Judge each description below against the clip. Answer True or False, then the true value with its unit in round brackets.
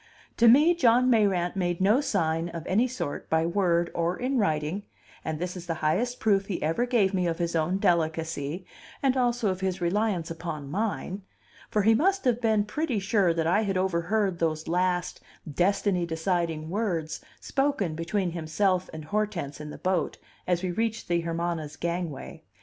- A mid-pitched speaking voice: True (180 Hz)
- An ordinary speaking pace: True (175 wpm)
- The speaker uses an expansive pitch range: False (4.2 semitones)